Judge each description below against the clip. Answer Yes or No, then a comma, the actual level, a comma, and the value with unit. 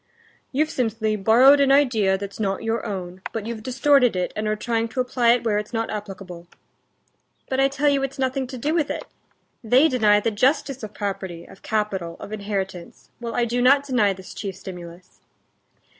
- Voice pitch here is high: Yes, high, 225 Hz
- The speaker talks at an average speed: Yes, average, 190 wpm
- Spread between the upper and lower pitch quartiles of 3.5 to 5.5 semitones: Yes, average, 4.5 semitones